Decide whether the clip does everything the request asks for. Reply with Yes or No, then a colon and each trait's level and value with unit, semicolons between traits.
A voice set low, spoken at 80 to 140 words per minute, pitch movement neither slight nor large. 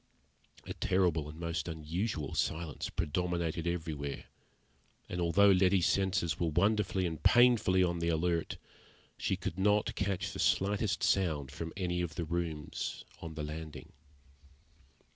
Yes: very low, 85 Hz; slow, 135 wpm; average, 3.0 semitones